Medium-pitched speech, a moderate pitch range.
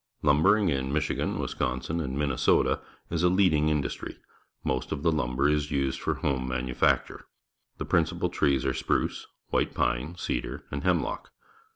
No: very low, 70 Hz; average, 3.2 semitones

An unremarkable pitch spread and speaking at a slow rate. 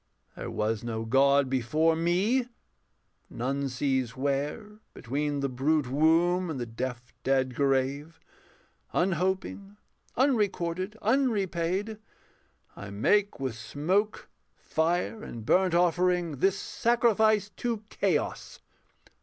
No: wide, 6.7 semitones; slow, 105 wpm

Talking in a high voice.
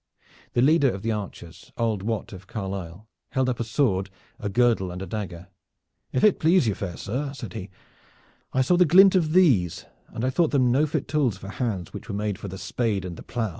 No: low, 115 Hz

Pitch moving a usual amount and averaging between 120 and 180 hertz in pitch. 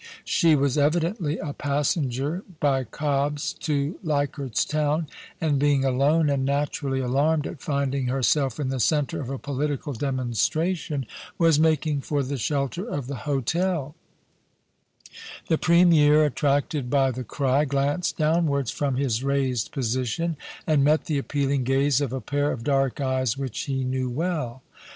No: narrow, 2.3 semitones; medium, 140 Hz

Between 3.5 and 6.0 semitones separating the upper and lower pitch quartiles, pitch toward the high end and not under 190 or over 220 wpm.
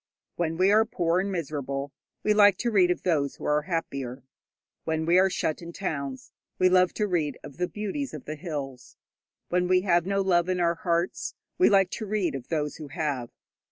No: average, 4.1 semitones; medium, 175 Hz; fast, 205 wpm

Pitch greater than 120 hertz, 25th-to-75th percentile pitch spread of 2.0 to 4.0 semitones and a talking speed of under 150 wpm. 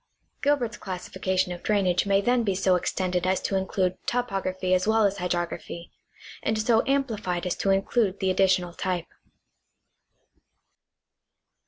Yes: high, 190 Hz; average, 2.9 semitones; slow, 135 wpm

